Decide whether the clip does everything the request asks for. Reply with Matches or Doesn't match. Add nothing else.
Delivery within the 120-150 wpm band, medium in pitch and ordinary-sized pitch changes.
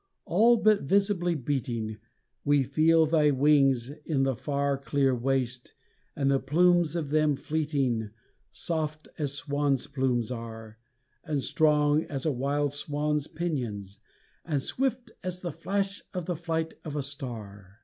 Matches